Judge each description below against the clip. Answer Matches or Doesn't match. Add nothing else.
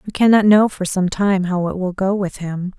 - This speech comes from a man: Doesn't match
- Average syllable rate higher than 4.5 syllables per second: Matches